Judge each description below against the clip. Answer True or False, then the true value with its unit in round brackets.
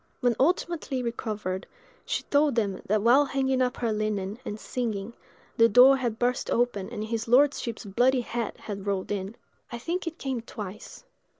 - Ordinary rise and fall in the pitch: True (3.6 semitones)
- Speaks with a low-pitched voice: False (235 Hz)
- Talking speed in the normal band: True (170 wpm)